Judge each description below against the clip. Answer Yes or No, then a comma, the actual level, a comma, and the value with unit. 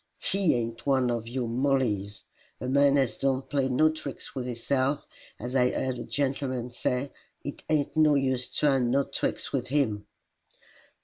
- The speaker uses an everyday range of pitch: No, narrow, 2.3 semitones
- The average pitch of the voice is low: Yes, low, 130 Hz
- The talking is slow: No, average, 165 wpm